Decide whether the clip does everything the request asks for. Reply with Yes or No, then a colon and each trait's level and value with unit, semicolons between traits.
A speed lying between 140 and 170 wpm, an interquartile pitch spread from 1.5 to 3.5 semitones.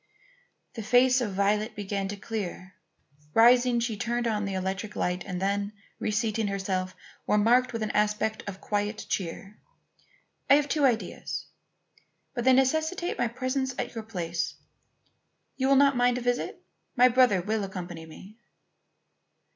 No: average, 145 wpm; average, 3.9 semitones